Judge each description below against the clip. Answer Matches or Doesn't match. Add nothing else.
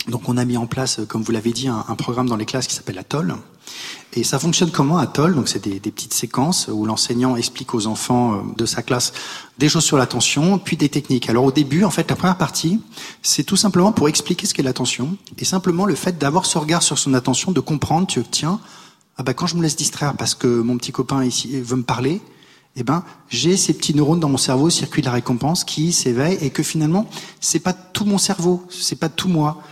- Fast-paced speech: Matches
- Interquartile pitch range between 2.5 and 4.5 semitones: Doesn't match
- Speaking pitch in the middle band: Matches